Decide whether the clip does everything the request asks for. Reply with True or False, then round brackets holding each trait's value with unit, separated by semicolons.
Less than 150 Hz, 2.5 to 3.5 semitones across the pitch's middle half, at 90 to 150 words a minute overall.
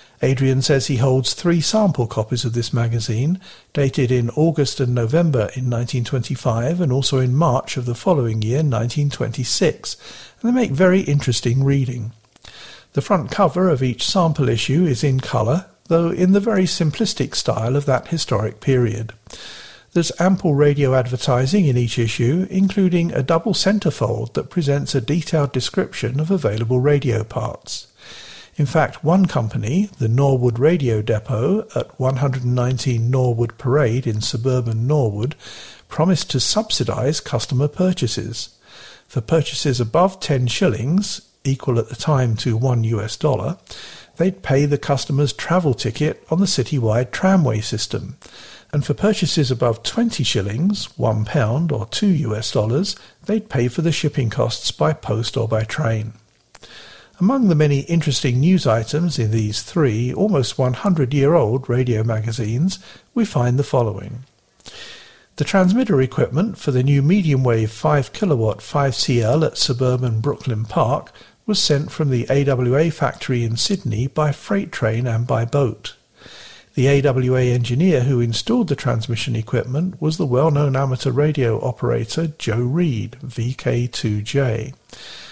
False (135 Hz; 4.7 semitones; 145 wpm)